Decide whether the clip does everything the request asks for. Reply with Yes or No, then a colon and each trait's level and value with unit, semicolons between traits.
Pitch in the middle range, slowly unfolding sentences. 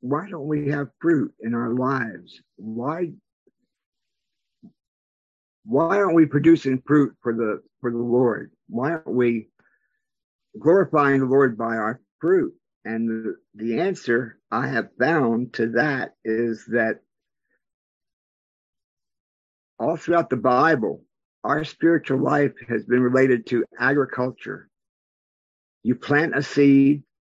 No: low, 130 Hz; slow, 120 wpm